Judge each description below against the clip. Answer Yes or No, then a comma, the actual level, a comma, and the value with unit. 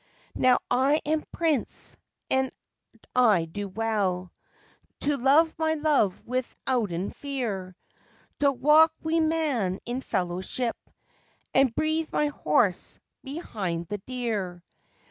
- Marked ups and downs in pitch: Yes, wide, 7.0 semitones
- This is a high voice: Yes, very high, 255 Hz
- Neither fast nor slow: No, slow, 105 wpm